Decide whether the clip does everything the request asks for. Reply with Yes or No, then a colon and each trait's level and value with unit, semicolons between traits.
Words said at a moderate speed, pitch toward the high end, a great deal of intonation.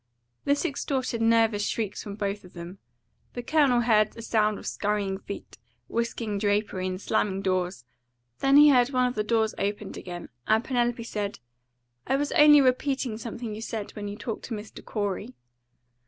No: average, 170 wpm; high, 220 Hz; average, 3.2 semitones